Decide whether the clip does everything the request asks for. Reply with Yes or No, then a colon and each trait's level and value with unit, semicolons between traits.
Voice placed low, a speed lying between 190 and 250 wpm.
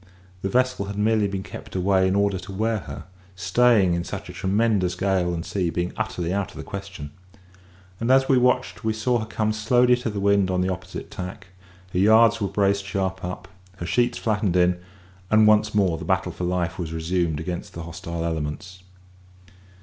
Yes: very low, 95 Hz; average, 195 wpm